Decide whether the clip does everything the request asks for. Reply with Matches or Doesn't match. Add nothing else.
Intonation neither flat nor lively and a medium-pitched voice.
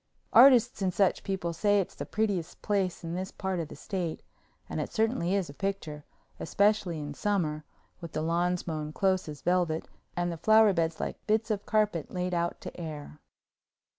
Matches